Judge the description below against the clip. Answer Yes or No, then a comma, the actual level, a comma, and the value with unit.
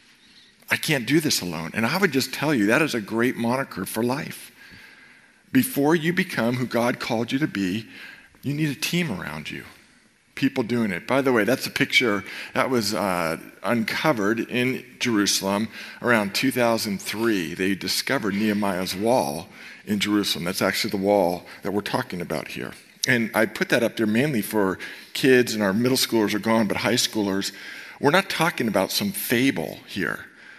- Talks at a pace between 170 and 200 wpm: Yes, average, 175 wpm